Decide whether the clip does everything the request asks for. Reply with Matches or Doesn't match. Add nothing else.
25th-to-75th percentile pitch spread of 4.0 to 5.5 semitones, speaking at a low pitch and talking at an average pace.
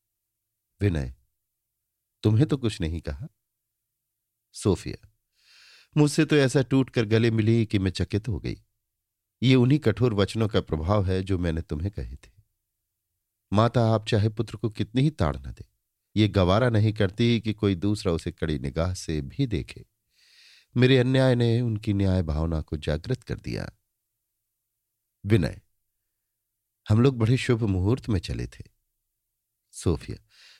Doesn't match